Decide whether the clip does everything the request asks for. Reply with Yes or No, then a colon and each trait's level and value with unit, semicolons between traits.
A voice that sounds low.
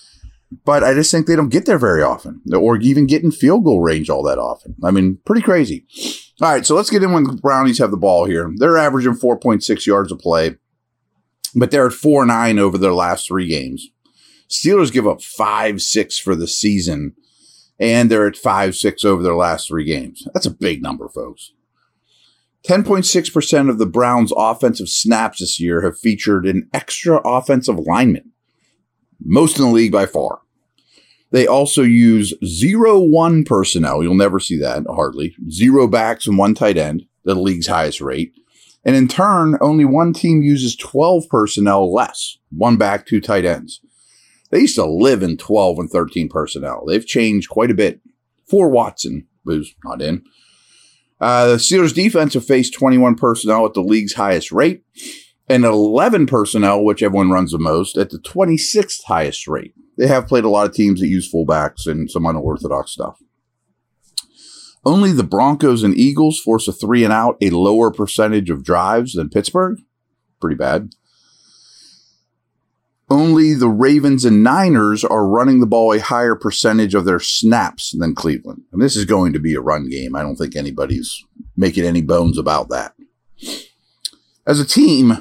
Yes: low, 115 Hz